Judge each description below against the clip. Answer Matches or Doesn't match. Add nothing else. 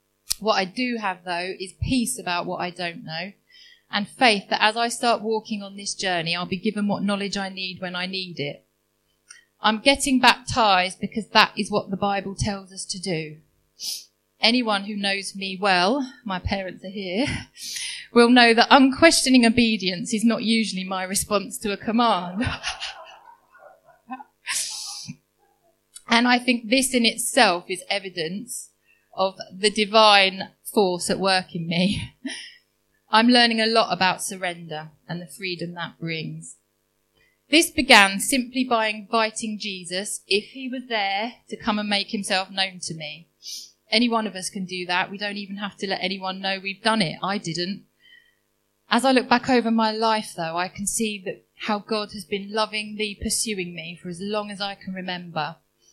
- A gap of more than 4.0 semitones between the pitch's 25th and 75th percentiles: Doesn't match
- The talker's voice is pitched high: Matches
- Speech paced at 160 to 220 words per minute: Matches